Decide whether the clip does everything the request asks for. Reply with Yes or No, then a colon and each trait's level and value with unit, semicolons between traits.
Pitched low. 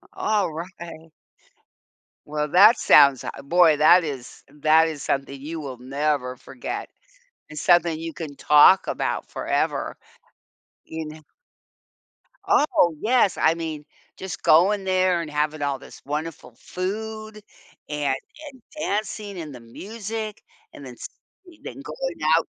No: medium, 160 Hz